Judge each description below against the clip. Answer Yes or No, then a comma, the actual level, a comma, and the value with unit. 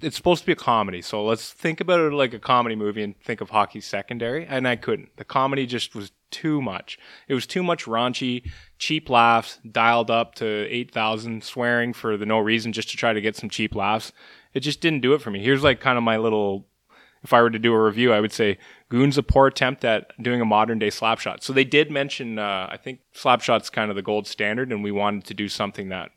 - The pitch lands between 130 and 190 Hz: No, low, 115 Hz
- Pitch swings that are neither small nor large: Yes, average, 3.7 semitones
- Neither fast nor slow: No, fast, 250 wpm